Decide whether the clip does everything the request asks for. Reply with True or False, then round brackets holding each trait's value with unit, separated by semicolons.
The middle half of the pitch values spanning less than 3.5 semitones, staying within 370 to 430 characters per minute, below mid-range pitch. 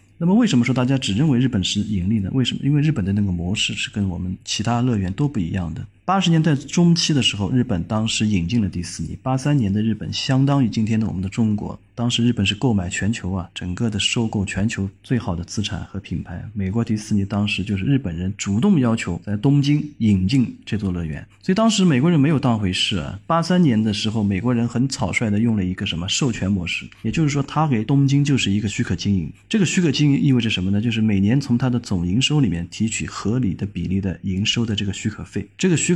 False (5.1 semitones; 375 characters per minute; 110 Hz)